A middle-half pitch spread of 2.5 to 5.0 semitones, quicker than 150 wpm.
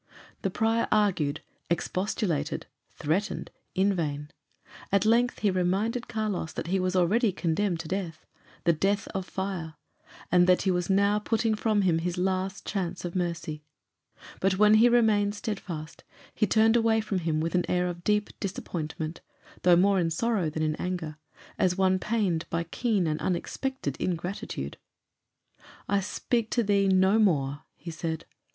Yes: average, 3.6 semitones; average, 160 wpm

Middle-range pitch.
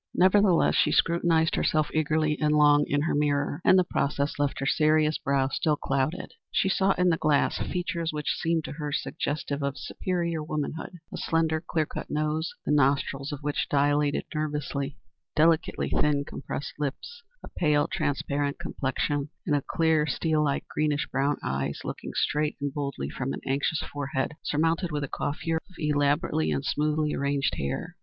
Yes: medium, 150 Hz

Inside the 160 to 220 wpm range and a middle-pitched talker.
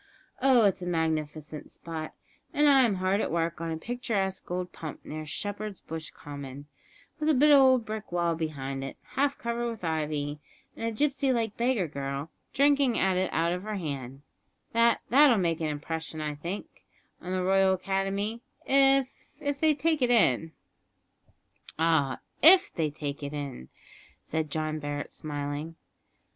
Yes: average, 165 wpm; medium, 180 Hz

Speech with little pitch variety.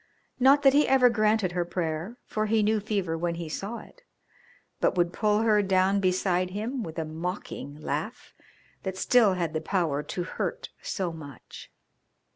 No: average, 4.3 semitones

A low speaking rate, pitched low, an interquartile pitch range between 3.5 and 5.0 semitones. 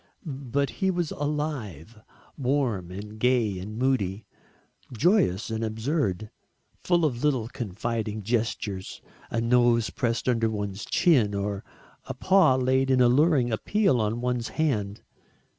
Yes: slow, 125 wpm; low, 120 Hz; average, 4.3 semitones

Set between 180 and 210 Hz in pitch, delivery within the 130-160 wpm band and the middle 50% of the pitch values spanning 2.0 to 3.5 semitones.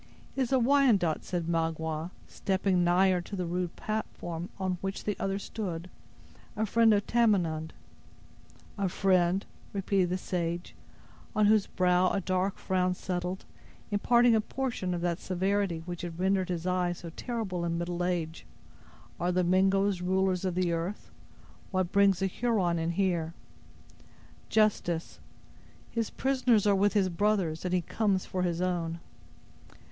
Yes: medium, 185 Hz; average, 150 wpm; narrow, 2.5 semitones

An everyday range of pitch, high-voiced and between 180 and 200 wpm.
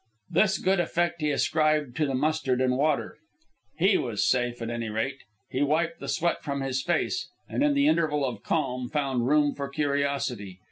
No: average, 3.4 semitones; medium, 140 Hz; average, 185 wpm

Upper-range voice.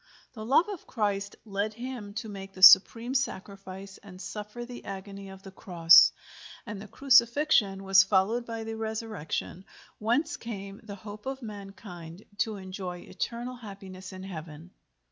Yes: high, 200 Hz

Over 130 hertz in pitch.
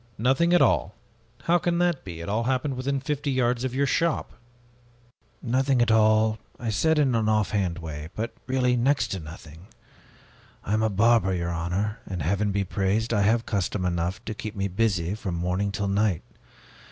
No: low, 110 Hz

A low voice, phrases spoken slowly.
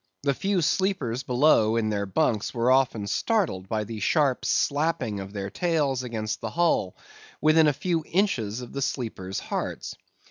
No: low, 125 Hz; average, 165 wpm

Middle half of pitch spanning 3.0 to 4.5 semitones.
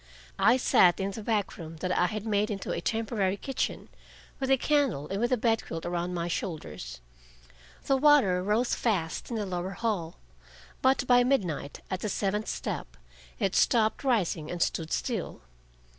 No: average, 5.1 semitones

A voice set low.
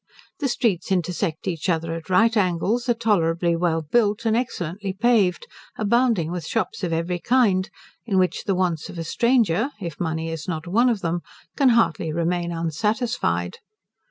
No: medium, 180 Hz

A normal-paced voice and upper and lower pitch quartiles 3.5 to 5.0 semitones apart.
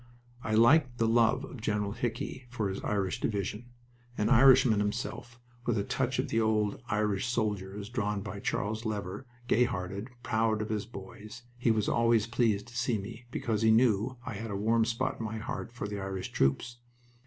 No: average, 190 wpm; narrow, 2.6 semitones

